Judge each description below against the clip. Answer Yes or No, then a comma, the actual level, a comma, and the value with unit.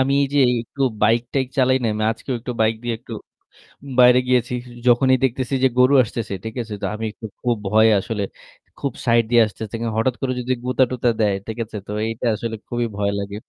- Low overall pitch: Yes, low, 120 Hz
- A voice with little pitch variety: Yes, narrow, 2.3 semitones